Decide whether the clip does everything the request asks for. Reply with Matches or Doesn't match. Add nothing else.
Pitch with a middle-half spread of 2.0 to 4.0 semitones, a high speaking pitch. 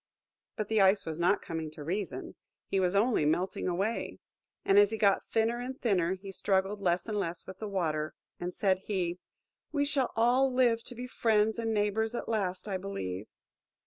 Matches